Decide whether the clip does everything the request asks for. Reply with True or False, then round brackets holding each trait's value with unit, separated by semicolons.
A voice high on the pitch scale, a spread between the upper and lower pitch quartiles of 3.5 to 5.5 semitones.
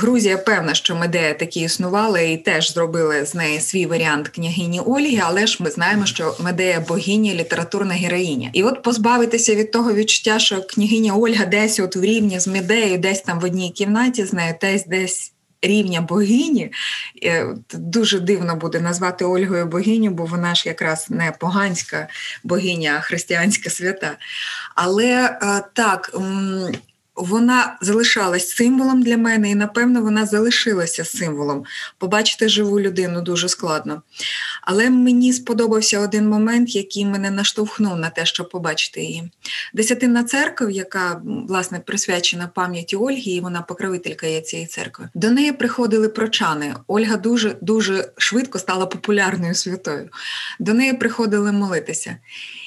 True (195 Hz; 4.0 semitones)